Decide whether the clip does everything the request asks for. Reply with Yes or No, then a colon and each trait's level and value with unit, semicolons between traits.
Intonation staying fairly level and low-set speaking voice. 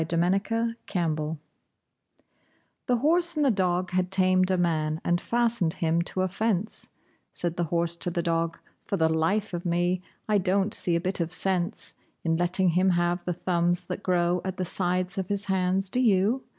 No: narrow, 2.1 semitones; medium, 180 Hz